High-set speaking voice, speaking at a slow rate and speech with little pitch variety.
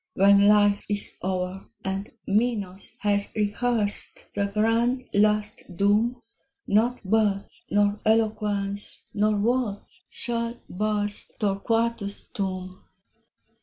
Yes: high, 205 Hz; slow, 95 wpm; narrow, 1.9 semitones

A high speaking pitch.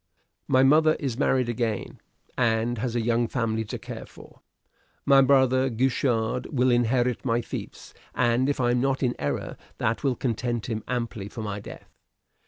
No: low, 120 Hz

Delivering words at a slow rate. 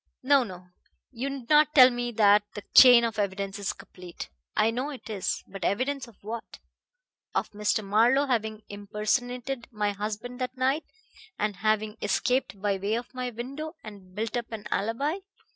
No: average, 165 wpm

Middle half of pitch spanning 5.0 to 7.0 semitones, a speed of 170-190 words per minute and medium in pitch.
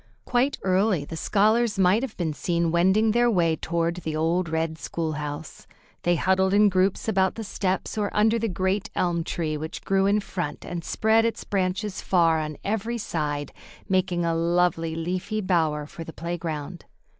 No: average, 3.6 semitones; average, 175 wpm; medium, 180 Hz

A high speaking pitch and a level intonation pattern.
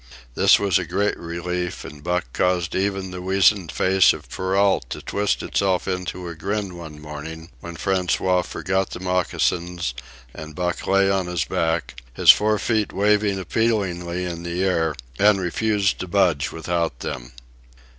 No: very low, 90 Hz; narrow, 2.3 semitones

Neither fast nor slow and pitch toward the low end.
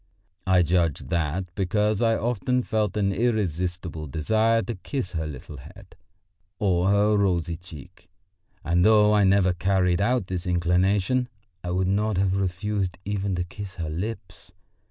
Yes: average, 150 wpm; very low, 95 Hz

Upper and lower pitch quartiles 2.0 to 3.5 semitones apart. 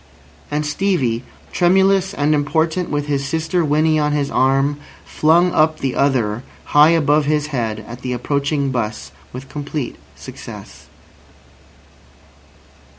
Yes: average, 2.7 semitones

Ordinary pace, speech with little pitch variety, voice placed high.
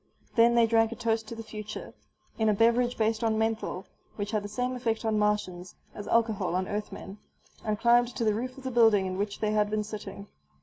No: fast, 220 wpm; narrow, 1.9 semitones; high, 220 Hz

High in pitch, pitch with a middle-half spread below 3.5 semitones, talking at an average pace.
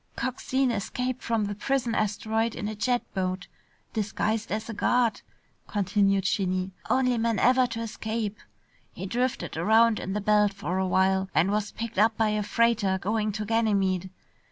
Yes: high, 215 Hz; average, 2.7 semitones; average, 165 wpm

